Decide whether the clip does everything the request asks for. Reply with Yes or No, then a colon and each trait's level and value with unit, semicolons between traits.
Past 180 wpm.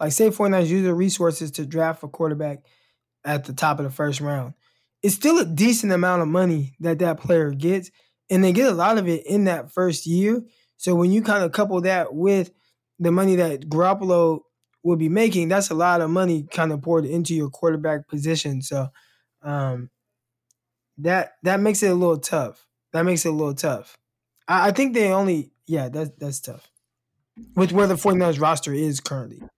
Yes: average, 195 wpm